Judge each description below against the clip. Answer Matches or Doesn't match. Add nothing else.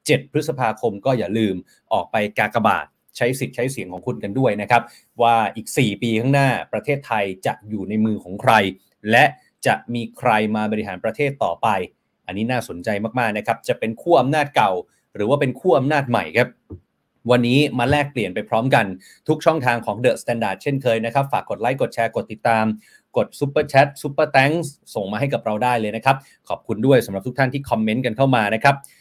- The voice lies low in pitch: Matches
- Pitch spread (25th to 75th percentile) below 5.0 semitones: Matches